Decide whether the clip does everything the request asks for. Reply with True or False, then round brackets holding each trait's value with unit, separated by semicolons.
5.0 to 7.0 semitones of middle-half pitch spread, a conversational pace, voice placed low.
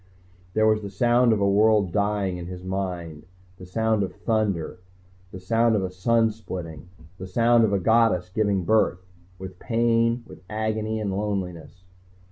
False (3.3 semitones; 165 wpm; 100 Hz)